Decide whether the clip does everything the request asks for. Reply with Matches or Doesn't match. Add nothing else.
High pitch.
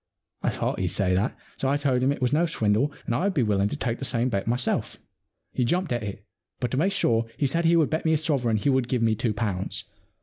Doesn't match